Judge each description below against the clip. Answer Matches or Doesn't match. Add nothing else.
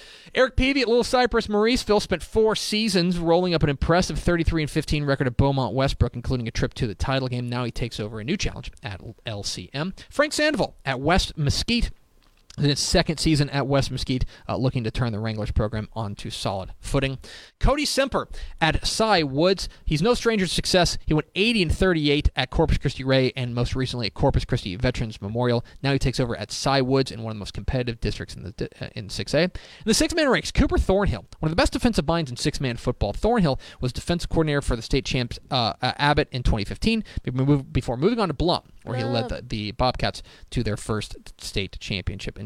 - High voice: Doesn't match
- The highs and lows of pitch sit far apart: Matches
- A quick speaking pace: Matches